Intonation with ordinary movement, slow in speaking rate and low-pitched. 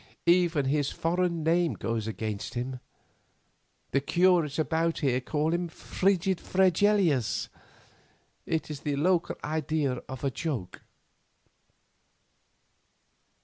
No: average, 4.3 semitones; slow, 105 wpm; medium, 155 Hz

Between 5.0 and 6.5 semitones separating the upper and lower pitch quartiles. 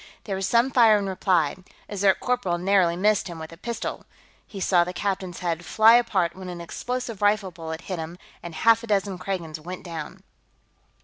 No: average, 3.4 semitones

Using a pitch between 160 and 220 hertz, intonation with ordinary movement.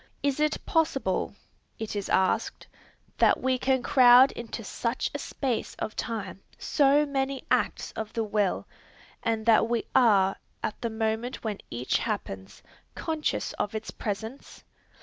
No: high, 230 Hz; average, 3.7 semitones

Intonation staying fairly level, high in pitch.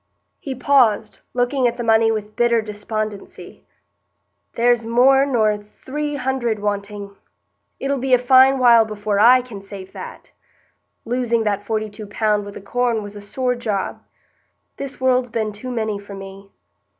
No: average, 3.3 semitones; high, 225 Hz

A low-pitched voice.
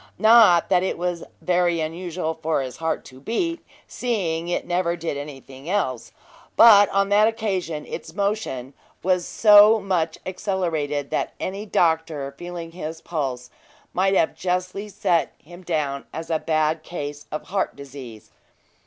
No: medium, 170 Hz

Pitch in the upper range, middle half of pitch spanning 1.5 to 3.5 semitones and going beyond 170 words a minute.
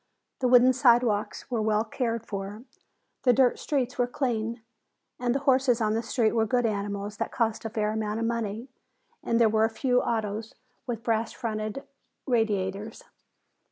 No: high, 225 Hz; narrow, 2.4 semitones; average, 160 wpm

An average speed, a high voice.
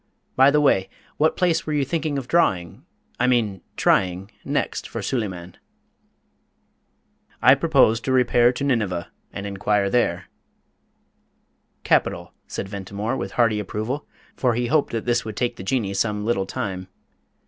No: average, 150 wpm; low, 115 Hz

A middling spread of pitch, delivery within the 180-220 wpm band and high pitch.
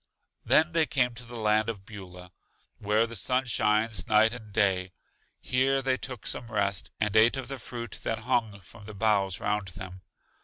No: average, 3.3 semitones; average, 185 wpm; low, 110 Hz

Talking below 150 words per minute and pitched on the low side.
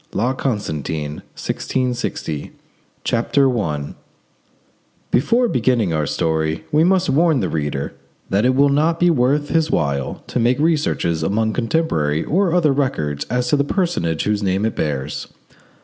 Yes: average, 140 wpm; low, 120 Hz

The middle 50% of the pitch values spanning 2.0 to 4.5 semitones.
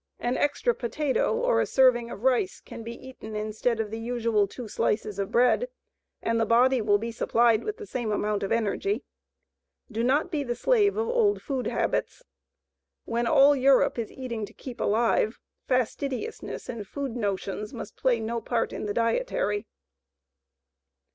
Yes: average, 3.5 semitones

